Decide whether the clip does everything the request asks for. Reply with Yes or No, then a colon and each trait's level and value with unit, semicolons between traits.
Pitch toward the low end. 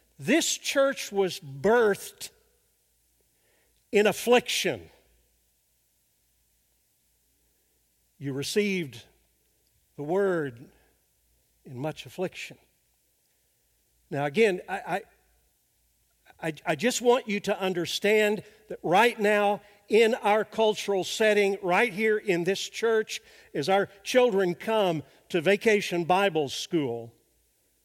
No: high, 195 Hz